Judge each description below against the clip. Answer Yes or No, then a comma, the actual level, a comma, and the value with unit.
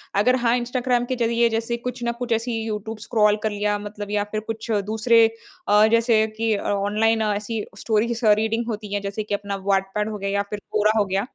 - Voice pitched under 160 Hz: No, high, 220 Hz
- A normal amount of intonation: No, narrow, 2.0 semitones